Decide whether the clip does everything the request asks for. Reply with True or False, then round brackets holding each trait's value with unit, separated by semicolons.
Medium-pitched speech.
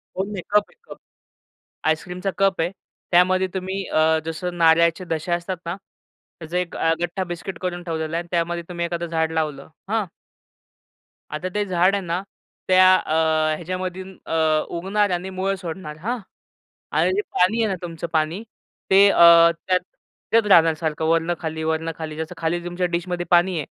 True (175 Hz)